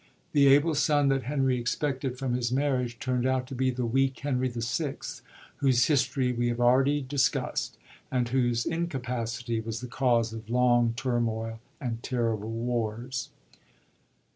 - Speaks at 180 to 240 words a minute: No, average, 150 wpm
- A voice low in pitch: Yes, low, 125 Hz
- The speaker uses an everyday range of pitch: No, narrow, 2.1 semitones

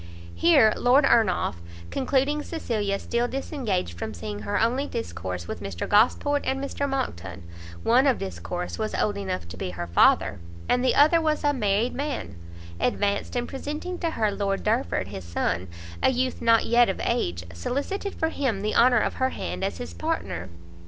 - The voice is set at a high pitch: Yes, high, 225 Hz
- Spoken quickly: No, average, 175 wpm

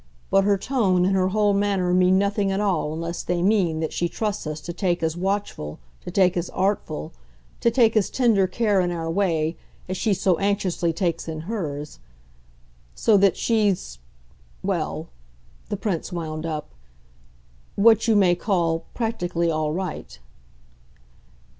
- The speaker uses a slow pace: No, average, 155 wpm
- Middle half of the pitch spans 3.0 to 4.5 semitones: Yes, average, 3.5 semitones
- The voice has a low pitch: No, medium, 185 Hz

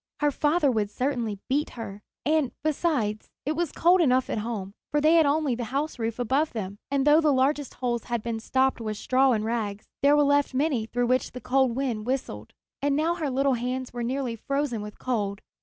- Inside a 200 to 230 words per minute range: Yes, fast, 205 wpm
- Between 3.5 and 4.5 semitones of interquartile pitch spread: Yes, average, 4.0 semitones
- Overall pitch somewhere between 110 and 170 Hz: No, very high, 260 Hz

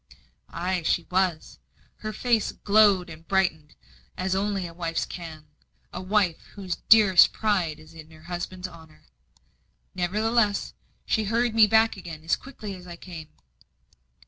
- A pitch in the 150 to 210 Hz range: Yes, medium, 185 Hz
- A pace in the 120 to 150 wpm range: Yes, average, 145 wpm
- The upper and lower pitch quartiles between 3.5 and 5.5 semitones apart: Yes, average, 3.9 semitones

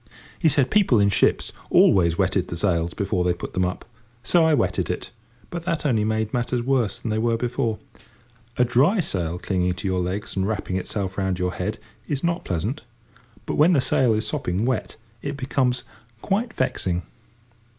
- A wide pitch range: Yes, wide, 6.3 semitones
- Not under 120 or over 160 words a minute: No, average, 185 wpm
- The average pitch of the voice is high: No, low, 110 Hz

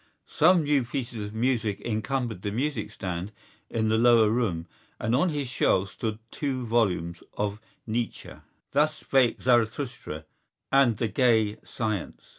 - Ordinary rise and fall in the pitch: Yes, average, 3.7 semitones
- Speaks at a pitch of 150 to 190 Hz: No, low, 115 Hz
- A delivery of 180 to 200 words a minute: No, average, 140 wpm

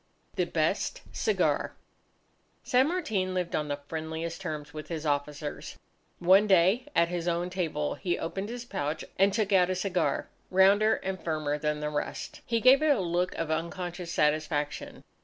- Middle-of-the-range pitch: Yes, medium, 175 Hz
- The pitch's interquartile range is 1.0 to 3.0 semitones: No, average, 4.1 semitones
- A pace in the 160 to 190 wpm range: Yes, average, 165 wpm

